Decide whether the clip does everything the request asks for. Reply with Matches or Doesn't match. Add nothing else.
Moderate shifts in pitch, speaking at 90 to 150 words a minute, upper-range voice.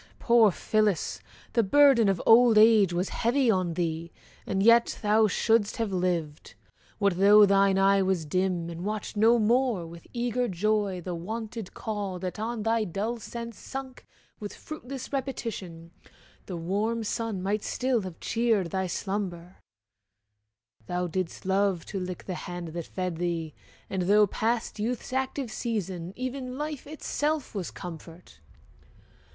Matches